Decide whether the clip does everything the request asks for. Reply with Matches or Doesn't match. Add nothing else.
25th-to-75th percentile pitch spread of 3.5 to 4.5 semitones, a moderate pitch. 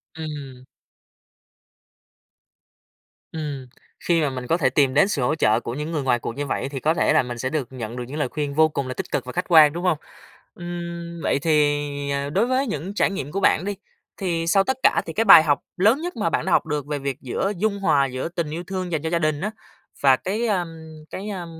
Matches